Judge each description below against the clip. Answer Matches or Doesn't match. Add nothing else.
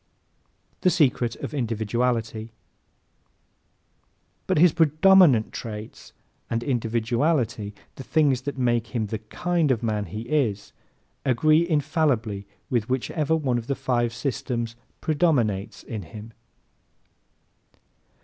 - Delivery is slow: Matches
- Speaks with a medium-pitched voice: Doesn't match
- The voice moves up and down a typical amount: Matches